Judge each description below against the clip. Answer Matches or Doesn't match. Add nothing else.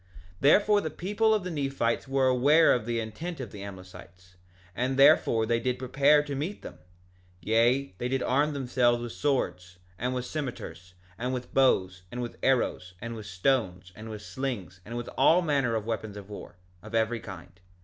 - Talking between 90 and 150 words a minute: Doesn't match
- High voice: Doesn't match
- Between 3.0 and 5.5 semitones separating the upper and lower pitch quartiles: Matches